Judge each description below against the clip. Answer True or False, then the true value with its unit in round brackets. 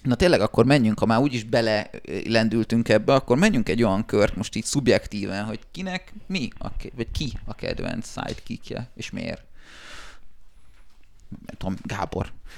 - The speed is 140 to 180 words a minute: True (155 wpm)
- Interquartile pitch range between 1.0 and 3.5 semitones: False (4.4 semitones)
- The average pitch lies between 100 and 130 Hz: True (110 Hz)